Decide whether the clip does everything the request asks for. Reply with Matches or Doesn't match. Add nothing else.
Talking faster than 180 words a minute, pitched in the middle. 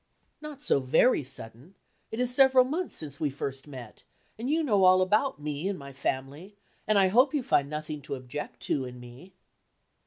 Matches